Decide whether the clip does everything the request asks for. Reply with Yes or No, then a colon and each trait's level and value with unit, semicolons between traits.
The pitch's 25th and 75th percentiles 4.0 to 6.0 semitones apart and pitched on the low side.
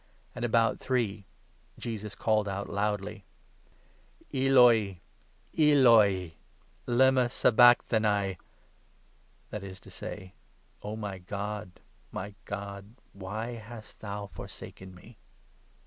No: average, 3.0 semitones; low, 105 Hz